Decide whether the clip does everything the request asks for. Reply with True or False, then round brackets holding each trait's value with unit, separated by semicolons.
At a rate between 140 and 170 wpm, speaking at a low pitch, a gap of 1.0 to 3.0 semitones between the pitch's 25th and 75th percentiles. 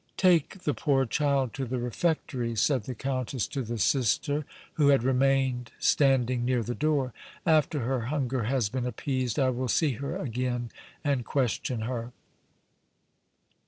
True (150 wpm; 130 Hz; 2.5 semitones)